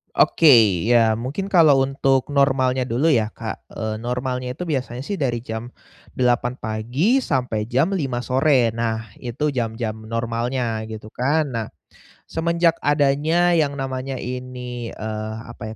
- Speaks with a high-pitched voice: No, low, 125 Hz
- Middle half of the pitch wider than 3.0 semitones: Yes, average, 3.5 semitones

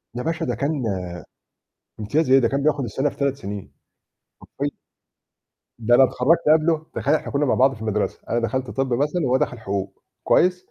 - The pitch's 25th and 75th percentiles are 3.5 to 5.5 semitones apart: Yes, average, 3.8 semitones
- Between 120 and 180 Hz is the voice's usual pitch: Yes, low, 135 Hz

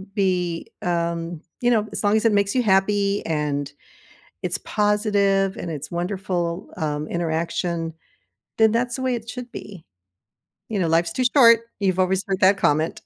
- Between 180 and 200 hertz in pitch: Yes, high, 190 Hz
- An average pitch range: Yes, average, 3.7 semitones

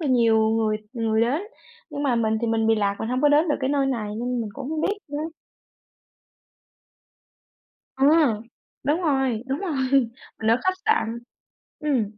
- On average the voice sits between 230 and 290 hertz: Yes, very high, 250 Hz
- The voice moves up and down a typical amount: Yes, average, 4.6 semitones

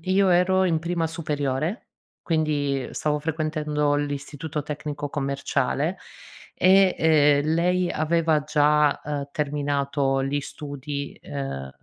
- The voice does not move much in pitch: Yes, narrow, 2.2 semitones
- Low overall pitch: No, medium, 150 Hz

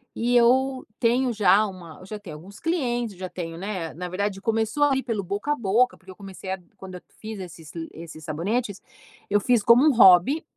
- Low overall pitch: No, high, 205 Hz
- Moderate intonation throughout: Yes, average, 4.8 semitones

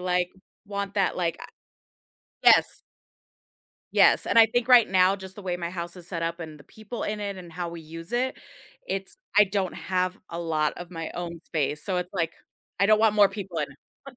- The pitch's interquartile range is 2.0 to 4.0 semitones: Yes, average, 3.1 semitones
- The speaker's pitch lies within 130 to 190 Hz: Yes, medium, 185 Hz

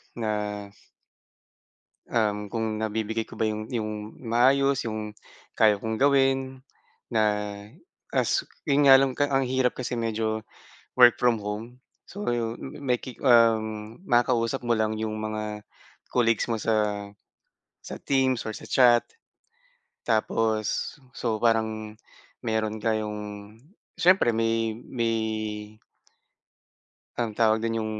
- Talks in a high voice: No, low, 115 Hz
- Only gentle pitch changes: Yes, narrow, 2.1 semitones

